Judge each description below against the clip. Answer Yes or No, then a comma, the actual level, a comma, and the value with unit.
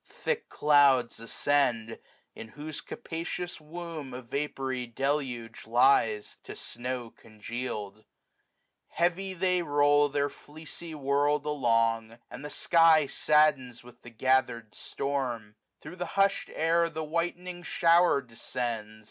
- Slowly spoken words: Yes, slow, 120 wpm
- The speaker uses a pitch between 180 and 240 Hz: No, medium, 140 Hz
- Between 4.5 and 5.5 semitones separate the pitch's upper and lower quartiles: Yes, average, 5.2 semitones